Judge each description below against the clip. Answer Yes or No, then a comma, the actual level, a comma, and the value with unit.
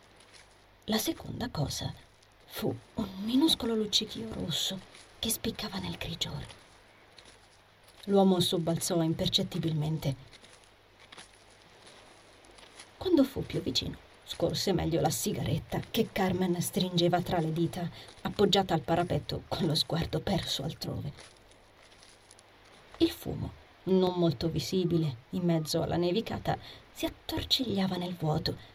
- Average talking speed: No, slow, 105 wpm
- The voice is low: No, medium, 170 Hz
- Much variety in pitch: Yes, wide, 8.1 semitones